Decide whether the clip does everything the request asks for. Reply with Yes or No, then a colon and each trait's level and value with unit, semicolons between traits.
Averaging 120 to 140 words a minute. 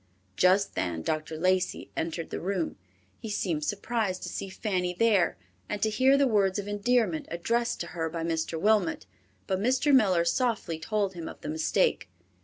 No: average, 175 wpm